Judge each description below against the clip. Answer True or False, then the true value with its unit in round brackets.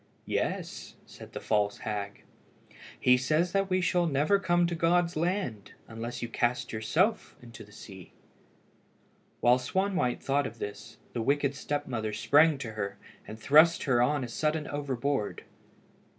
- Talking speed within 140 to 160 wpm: True (150 wpm)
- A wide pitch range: True (6.3 semitones)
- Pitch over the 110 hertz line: True (135 Hz)